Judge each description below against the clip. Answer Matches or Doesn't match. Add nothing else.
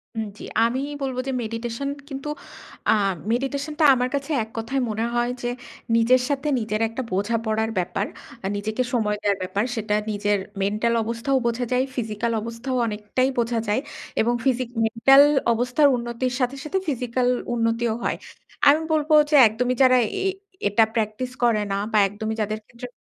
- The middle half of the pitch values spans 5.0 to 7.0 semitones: Doesn't match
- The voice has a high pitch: Matches